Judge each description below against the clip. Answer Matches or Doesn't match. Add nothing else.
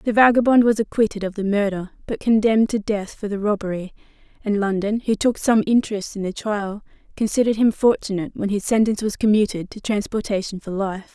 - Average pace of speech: Matches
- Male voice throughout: Doesn't match